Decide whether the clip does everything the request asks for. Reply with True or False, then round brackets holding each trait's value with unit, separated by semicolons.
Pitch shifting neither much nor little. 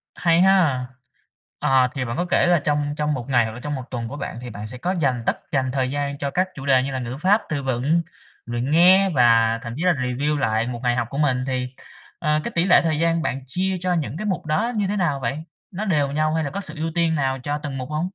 True (4.6 semitones)